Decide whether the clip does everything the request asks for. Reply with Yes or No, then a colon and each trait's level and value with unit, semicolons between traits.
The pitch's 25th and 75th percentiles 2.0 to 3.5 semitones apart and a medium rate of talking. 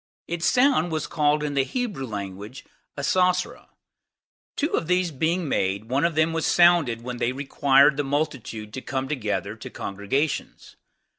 No: average, 4.9 semitones; average, 155 wpm